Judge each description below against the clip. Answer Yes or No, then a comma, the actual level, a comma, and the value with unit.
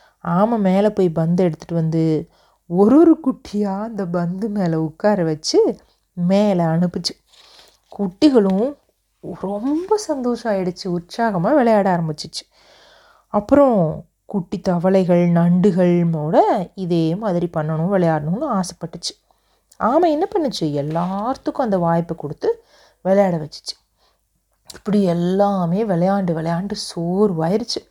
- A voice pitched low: No, high, 190 Hz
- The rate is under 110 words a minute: Yes, average, 100 wpm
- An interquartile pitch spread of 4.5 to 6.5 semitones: No, average, 3.8 semitones